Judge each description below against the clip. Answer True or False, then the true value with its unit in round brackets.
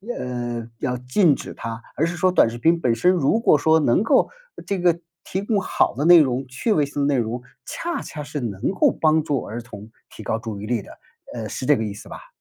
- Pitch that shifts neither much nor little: False (6.0 semitones)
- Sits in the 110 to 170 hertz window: True (135 Hz)